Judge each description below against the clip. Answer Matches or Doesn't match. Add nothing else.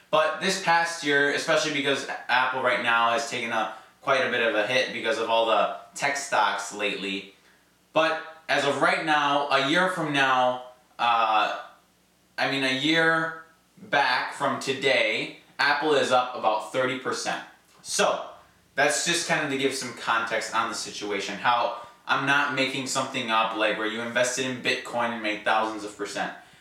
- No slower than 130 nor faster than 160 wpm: Doesn't match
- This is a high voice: Doesn't match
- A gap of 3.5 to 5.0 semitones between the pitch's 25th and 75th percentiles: Matches